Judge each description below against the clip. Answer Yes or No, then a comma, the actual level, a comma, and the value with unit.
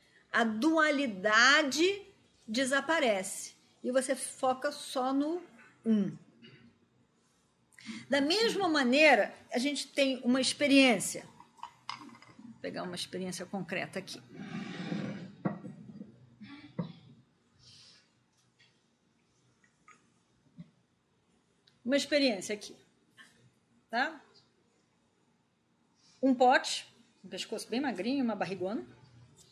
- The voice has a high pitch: Yes, high, 225 Hz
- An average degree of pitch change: No, wide, 6.9 semitones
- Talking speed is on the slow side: Yes, slow, 70 wpm